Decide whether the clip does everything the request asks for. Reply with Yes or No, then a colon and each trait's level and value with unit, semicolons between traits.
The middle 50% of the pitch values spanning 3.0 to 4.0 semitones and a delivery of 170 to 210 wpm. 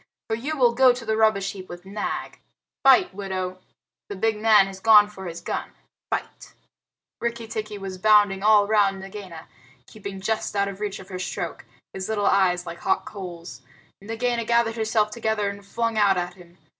No: narrow, 2.5 semitones; average, 180 wpm